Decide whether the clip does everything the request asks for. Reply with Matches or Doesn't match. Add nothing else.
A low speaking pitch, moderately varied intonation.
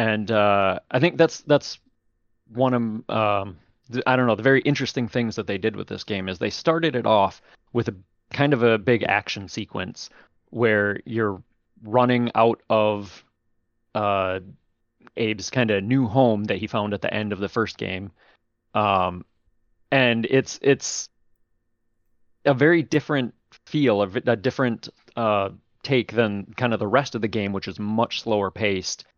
Matches